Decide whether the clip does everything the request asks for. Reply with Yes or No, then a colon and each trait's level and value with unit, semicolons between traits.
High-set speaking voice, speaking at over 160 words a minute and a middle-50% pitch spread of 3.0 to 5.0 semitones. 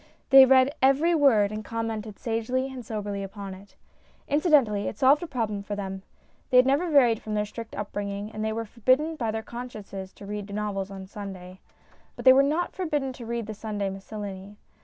Yes: high, 220 Hz; average, 200 wpm; average, 4.3 semitones